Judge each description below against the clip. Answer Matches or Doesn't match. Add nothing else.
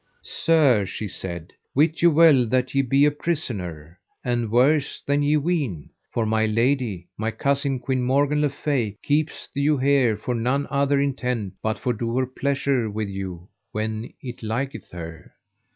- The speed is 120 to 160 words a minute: Doesn't match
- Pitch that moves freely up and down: Doesn't match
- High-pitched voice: Doesn't match